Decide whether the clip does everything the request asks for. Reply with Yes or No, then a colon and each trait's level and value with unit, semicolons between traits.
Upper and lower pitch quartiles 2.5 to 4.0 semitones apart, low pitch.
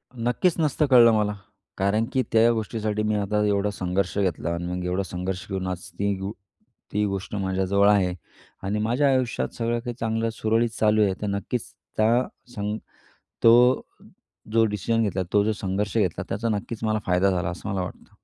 Yes: average, 3.0 semitones; low, 105 Hz